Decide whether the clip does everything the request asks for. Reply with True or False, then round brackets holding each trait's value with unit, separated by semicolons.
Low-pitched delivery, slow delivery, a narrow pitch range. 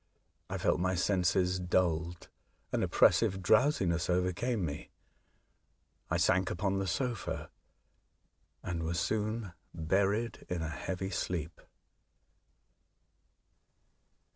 True (90 Hz; 100 wpm; 2.3 semitones)